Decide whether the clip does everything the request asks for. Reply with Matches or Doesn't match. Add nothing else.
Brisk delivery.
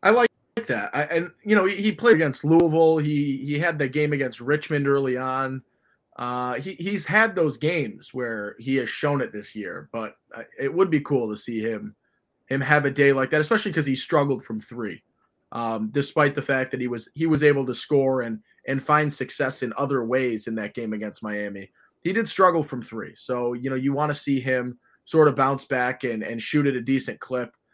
Matches